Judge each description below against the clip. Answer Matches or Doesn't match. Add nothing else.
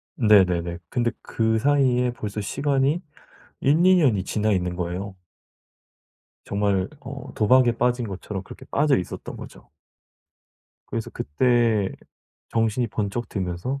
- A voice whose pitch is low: Matches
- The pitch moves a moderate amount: Matches